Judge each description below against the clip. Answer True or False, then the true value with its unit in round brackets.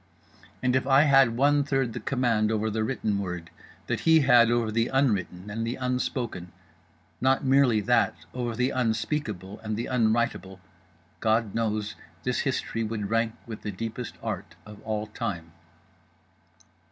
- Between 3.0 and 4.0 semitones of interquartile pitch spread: True (3.6 semitones)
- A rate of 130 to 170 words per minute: True (145 wpm)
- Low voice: True (115 Hz)